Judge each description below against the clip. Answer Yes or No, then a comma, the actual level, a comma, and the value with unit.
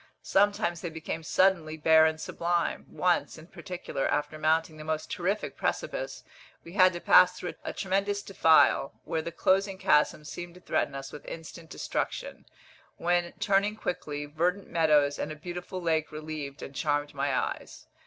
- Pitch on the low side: No, medium, 165 Hz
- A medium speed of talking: Yes, average, 165 wpm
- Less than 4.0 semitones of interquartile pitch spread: Yes, average, 2.9 semitones